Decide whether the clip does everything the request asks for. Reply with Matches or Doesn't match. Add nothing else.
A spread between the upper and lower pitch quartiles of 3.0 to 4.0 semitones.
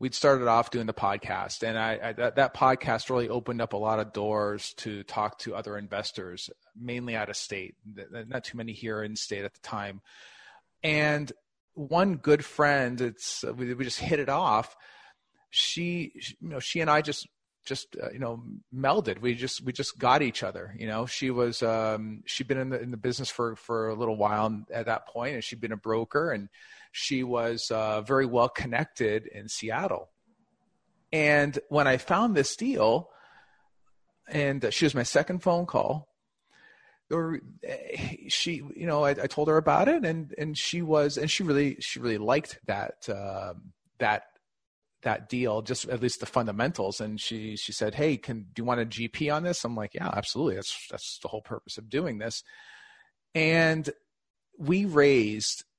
Doesn't match